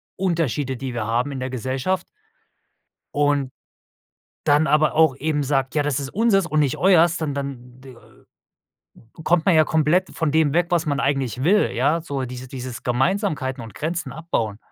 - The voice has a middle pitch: Yes, medium, 145 Hz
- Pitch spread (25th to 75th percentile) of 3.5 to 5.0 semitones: Yes, average, 3.9 semitones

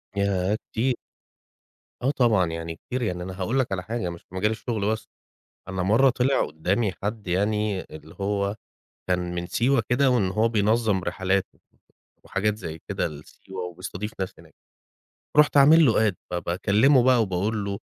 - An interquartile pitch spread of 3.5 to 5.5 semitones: Yes, average, 4.1 semitones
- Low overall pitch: Yes, low, 100 Hz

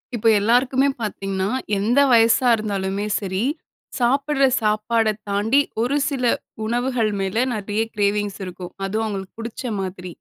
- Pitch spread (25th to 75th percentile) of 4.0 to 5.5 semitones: No, average, 3.5 semitones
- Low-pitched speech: No, high, 215 Hz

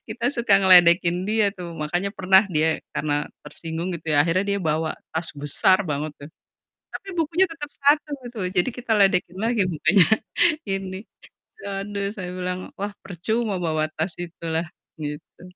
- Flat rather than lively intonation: No, average, 4.0 semitones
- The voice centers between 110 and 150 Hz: No, medium, 185 Hz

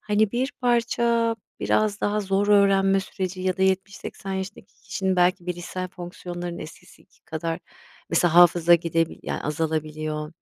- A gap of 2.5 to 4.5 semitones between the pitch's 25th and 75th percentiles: Yes, average, 3.0 semitones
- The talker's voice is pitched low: No, medium, 185 Hz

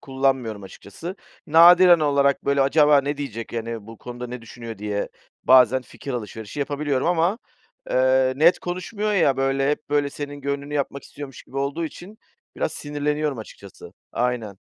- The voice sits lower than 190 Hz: Yes, medium, 140 Hz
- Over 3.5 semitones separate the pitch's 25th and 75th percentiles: No, average, 3.2 semitones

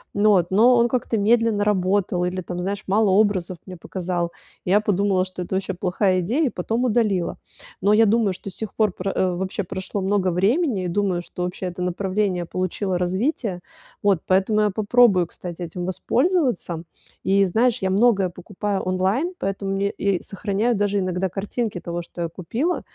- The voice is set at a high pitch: Yes, high, 195 Hz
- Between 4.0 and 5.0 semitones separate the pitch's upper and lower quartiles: No, average, 2.8 semitones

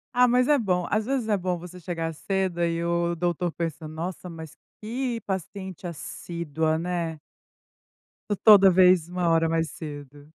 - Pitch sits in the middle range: Yes, medium, 175 Hz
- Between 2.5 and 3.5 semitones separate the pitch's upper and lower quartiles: Yes, average, 2.8 semitones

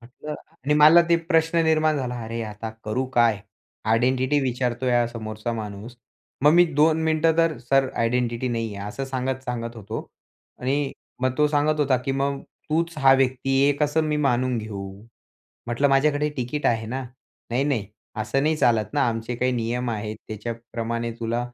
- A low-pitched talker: Yes, low, 125 Hz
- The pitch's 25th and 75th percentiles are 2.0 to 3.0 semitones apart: No, average, 4.0 semitones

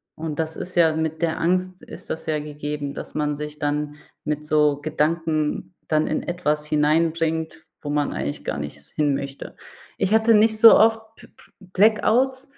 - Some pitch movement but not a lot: Yes, average, 3.0 semitones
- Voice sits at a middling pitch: Yes, medium, 155 Hz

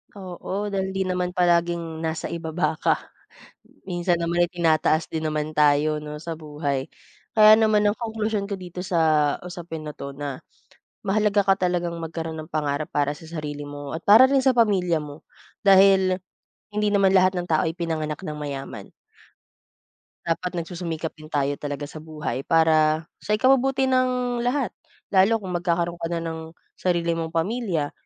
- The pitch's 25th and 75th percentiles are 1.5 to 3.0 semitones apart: No, average, 3.8 semitones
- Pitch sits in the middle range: Yes, medium, 170 Hz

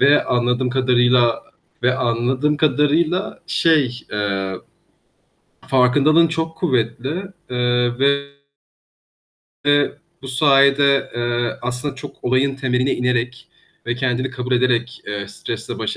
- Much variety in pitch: No, narrow, 2.5 semitones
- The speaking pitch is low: Yes, low, 125 Hz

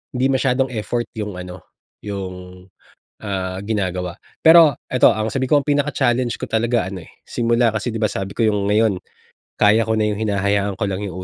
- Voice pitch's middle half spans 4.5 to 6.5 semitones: No, average, 3.7 semitones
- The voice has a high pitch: No, low, 110 Hz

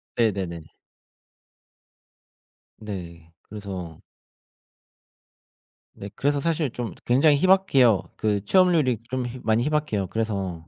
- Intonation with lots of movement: Yes, wide, 6.5 semitones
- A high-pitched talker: No, low, 110 Hz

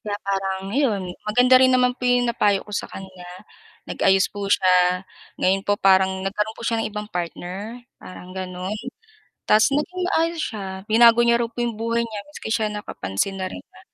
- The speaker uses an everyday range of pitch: Yes, average, 3.6 semitones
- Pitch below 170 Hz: No, high, 210 Hz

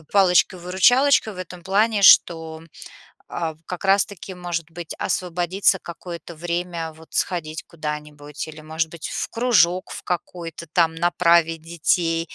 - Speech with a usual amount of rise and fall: No, narrow, 2.1 semitones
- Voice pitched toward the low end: No, medium, 170 Hz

